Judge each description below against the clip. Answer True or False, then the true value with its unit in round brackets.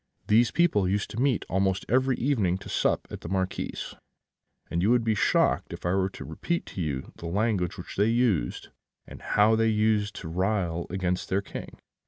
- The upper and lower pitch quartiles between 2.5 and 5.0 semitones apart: True (3.7 semitones)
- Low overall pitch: True (100 Hz)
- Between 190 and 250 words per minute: True (195 wpm)